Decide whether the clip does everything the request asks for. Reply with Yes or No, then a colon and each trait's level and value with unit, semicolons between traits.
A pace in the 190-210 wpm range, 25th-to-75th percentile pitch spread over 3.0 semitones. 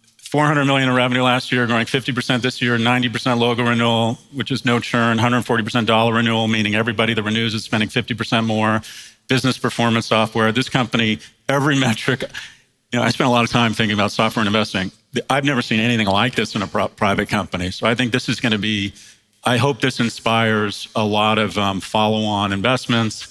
No: average, 200 wpm; narrow, 2.4 semitones